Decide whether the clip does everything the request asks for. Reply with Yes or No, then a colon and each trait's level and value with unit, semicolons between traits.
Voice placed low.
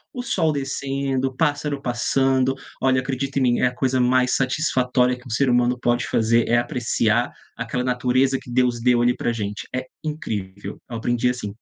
Yes: low, 125 Hz